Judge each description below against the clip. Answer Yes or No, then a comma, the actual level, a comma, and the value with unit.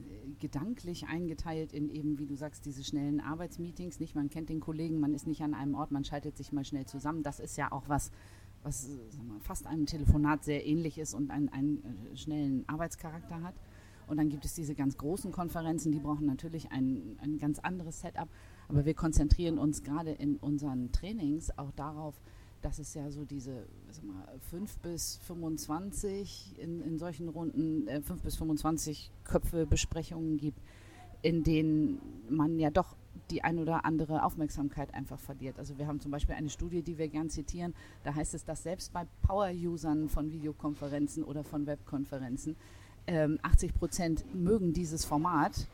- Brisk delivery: No, average, 175 wpm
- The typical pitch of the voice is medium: Yes, medium, 150 Hz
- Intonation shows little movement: Yes, narrow, 2.3 semitones